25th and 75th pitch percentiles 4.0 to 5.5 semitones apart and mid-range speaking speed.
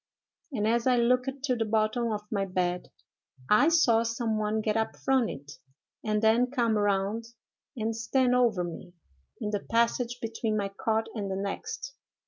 No: narrow, 2.6 semitones; average, 170 wpm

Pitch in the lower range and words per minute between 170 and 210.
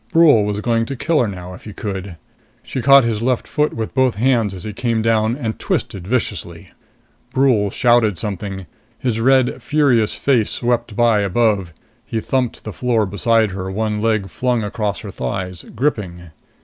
Yes: low, 110 Hz; average, 175 wpm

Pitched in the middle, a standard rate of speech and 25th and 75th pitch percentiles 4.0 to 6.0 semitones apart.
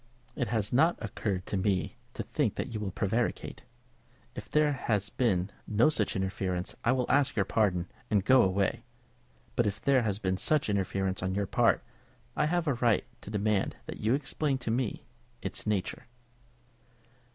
No: low, 105 Hz; average, 175 wpm; average, 4.6 semitones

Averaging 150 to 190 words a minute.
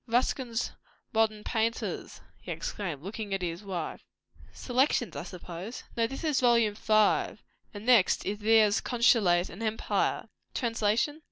No: average, 140 wpm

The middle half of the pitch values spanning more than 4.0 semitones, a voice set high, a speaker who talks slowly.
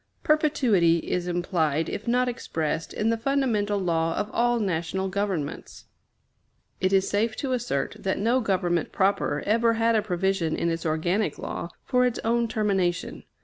No: average, 4.9 semitones; high, 200 Hz; average, 155 wpm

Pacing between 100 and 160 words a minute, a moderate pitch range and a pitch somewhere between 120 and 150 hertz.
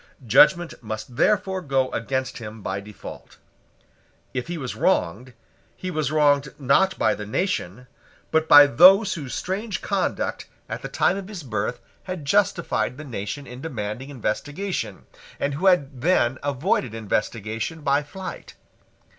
No: average, 145 wpm; wide, 7.1 semitones; medium, 140 Hz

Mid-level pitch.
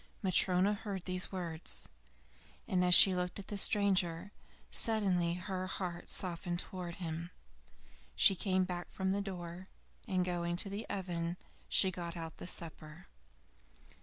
Yes: medium, 180 Hz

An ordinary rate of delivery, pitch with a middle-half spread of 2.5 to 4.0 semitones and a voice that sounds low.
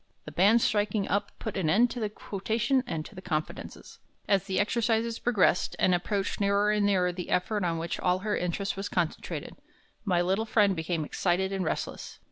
No: average, 190 wpm; average, 2.9 semitones; high, 195 Hz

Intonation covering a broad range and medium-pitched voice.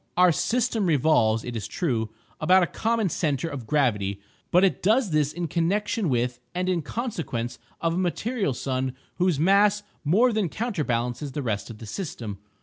Yes: wide, 7.7 semitones; medium, 165 Hz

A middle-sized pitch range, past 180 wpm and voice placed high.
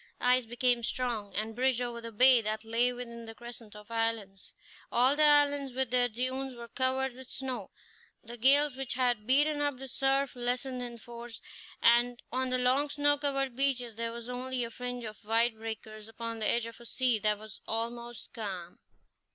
No: narrow, 2.3 semitones; average, 190 wpm; high, 245 Hz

